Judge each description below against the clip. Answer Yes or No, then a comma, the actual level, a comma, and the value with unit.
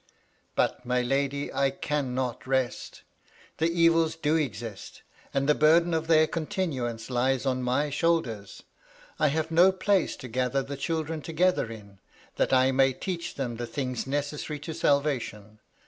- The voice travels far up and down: No, average, 4.2 semitones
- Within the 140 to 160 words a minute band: Yes, average, 155 wpm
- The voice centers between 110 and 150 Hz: Yes, medium, 140 Hz